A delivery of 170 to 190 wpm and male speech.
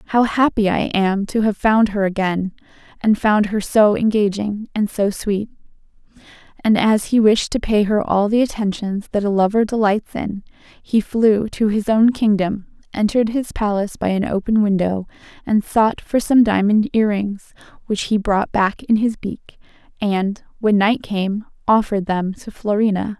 No: average, 175 wpm; female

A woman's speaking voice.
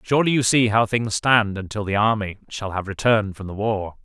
No: male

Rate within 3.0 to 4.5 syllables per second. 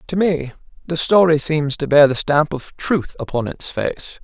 Yes: 4.4 syllables/s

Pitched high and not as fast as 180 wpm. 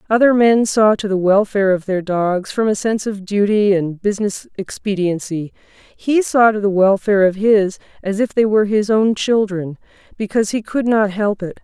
No: high, 205 Hz; average, 190 wpm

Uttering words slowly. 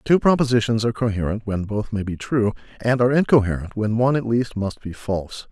No: fast, 205 wpm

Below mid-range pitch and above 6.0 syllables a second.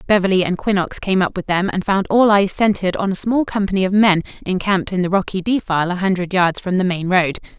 No: high, 190 Hz; 6.2 syllables/s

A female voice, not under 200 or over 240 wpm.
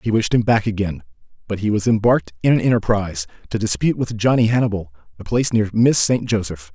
No: male; fast, 205 wpm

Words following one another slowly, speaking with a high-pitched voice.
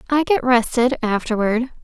Yes: slow, 100 wpm; high, 245 Hz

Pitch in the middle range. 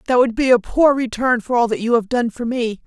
No: high, 240 Hz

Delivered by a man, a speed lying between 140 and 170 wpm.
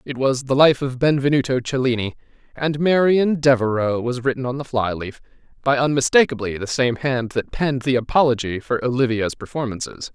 Yes: male; average, 165 wpm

